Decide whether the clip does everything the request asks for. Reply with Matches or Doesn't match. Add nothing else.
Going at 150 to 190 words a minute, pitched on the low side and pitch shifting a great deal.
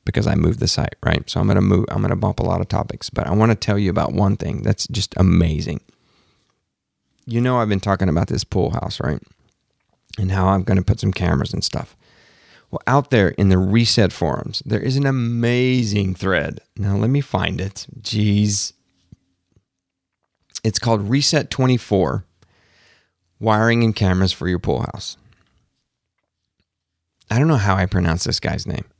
Doesn't match